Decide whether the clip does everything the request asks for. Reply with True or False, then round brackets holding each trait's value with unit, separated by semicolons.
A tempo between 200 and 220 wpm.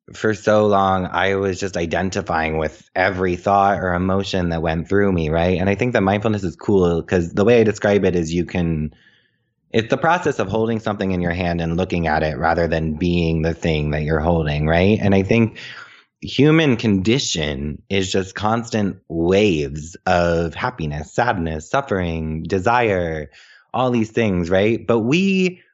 False (175 wpm)